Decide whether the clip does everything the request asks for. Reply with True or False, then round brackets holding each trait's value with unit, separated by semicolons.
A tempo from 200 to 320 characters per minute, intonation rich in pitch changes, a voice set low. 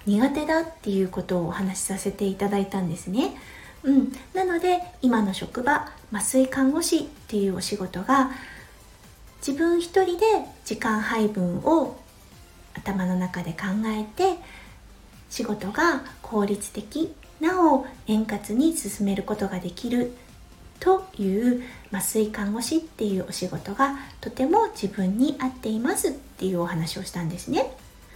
False (275 characters per minute; 6.9 semitones; 220 Hz)